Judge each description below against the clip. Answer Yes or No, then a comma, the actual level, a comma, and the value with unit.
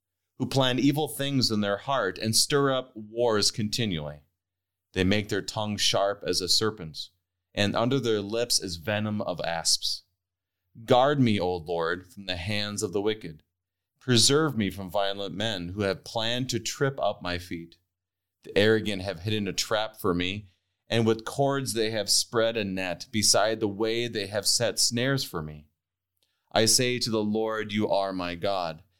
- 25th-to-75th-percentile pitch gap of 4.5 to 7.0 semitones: No, average, 3.8 semitones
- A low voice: Yes, low, 105 Hz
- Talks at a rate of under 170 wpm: No, average, 175 wpm